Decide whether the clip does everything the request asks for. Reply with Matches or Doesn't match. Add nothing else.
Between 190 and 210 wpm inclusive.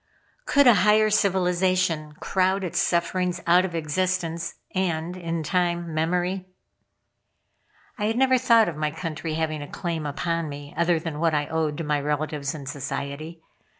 Doesn't match